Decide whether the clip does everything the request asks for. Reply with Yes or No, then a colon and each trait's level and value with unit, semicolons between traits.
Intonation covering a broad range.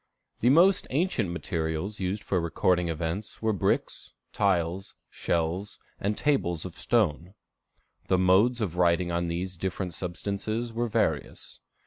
No: average, 3.9 semitones